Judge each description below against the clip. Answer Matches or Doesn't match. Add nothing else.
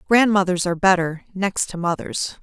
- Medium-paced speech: Matches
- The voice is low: Doesn't match